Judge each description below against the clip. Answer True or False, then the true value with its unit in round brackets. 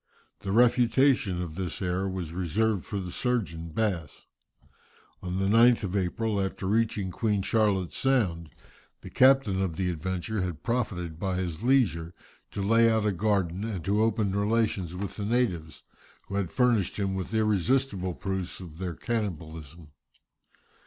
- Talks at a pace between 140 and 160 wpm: True (150 wpm)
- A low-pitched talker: True (95 Hz)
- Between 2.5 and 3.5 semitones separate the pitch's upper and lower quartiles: False (3.9 semitones)